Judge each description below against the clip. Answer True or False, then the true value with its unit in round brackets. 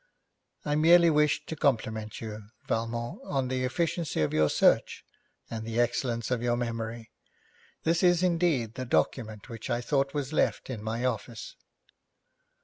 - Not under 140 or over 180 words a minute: True (150 wpm)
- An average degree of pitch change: True (4.5 semitones)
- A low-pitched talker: True (120 Hz)